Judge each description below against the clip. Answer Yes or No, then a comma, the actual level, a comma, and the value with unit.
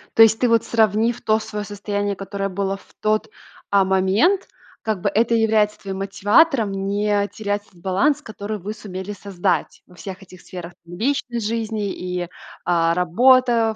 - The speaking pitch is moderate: No, high, 205 Hz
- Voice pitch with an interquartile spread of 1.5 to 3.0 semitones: Yes, narrow, 2.5 semitones